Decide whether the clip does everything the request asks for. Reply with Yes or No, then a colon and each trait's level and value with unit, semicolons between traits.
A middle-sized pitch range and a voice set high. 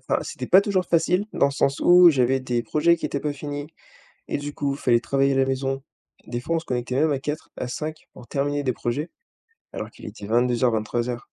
No: average, 3.5 semitones; medium, 140 Hz